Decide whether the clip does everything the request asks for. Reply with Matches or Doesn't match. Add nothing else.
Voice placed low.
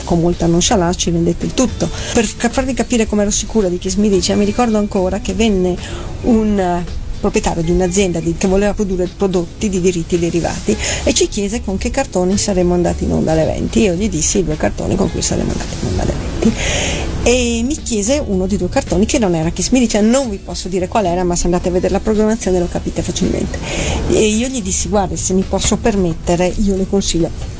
Doesn't match